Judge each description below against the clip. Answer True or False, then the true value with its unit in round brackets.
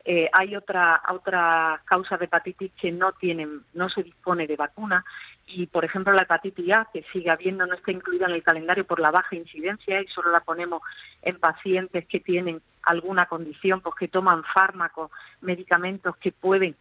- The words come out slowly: False (180 wpm)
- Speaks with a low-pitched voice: False (180 Hz)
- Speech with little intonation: True (1.9 semitones)